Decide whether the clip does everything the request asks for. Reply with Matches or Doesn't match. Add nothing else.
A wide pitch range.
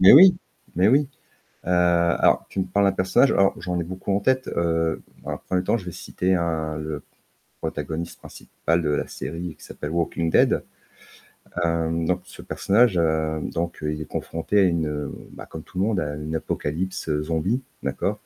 Doesn't match